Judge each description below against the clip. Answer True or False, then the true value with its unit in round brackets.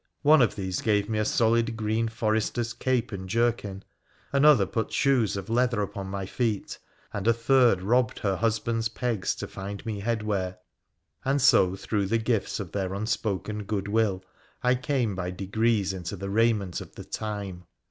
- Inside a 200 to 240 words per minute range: False (170 wpm)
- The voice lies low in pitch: True (110 Hz)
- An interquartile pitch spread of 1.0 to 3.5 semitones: True (3.0 semitones)